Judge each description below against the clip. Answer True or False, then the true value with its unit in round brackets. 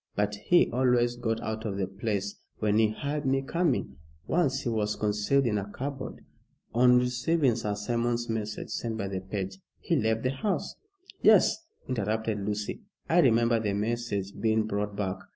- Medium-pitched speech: False (110 Hz)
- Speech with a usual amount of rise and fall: True (3.2 semitones)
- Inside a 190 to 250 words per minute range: False (170 wpm)